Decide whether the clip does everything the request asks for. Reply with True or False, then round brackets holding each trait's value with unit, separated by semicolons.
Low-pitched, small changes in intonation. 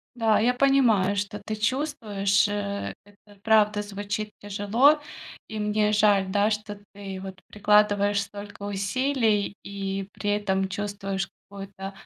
False (205 Hz; 1.1 semitones)